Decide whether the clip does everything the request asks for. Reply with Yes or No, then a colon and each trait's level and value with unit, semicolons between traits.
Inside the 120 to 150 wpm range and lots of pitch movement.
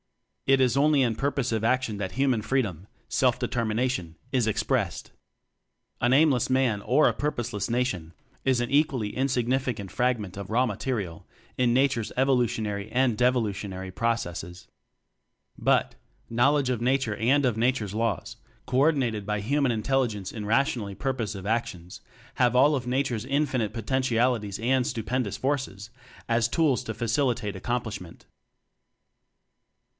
No: average, 140 wpm; average, 3.9 semitones